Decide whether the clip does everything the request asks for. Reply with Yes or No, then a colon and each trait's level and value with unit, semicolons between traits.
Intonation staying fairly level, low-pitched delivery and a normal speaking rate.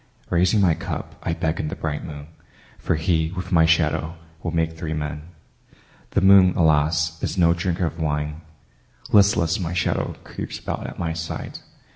Yes: narrow, 1.9 semitones; very low, 80 Hz; average, 165 wpm